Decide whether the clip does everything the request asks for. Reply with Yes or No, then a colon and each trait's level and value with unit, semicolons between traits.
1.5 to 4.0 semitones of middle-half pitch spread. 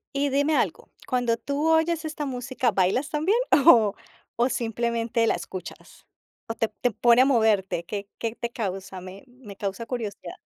No: average, 4.6 semitones